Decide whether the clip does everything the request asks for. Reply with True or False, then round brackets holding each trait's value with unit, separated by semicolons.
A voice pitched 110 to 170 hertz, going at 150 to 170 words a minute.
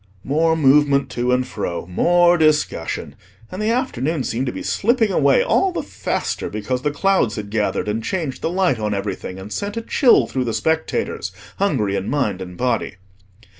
False (140 Hz; 180 wpm)